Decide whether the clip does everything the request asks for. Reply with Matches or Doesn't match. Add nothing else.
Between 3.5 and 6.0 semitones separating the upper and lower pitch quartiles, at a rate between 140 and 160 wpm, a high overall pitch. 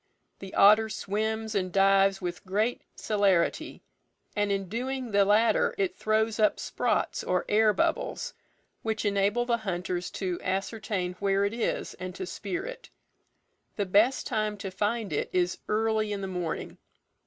Doesn't match